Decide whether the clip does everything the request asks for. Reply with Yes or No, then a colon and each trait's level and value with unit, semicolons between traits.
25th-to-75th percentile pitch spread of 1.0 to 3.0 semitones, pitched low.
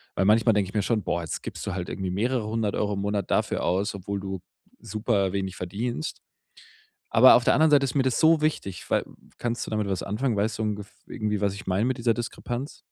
No: average, 3.4 semitones; low, 105 Hz